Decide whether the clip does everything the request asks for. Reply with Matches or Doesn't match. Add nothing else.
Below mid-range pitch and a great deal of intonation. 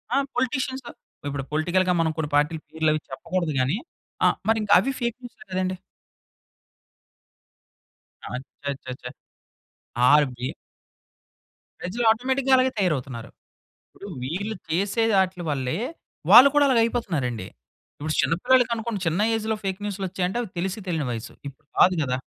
Doesn't match